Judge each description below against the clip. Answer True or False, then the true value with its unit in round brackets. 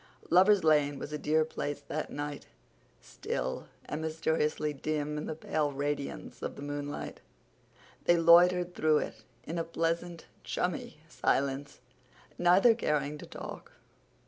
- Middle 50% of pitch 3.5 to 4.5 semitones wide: False (2.4 semitones)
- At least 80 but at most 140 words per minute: True (135 wpm)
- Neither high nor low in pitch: True (155 Hz)